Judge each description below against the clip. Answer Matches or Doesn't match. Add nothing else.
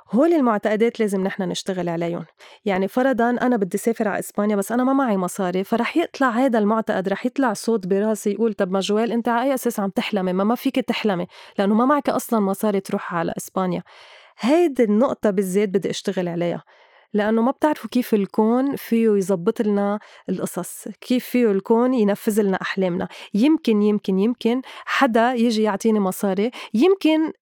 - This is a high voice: Matches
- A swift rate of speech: Matches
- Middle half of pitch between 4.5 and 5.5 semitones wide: Doesn't match